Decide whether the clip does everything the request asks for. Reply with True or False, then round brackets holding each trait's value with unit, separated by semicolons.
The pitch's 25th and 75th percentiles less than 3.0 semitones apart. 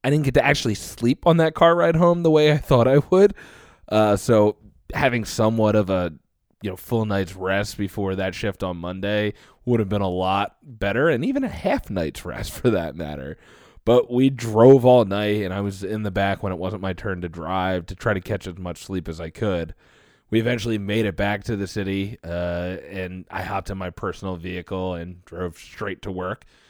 False (4.1 semitones)